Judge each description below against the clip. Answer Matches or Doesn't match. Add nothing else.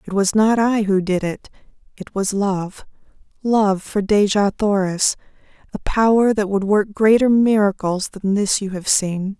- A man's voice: Doesn't match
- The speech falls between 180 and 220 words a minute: Doesn't match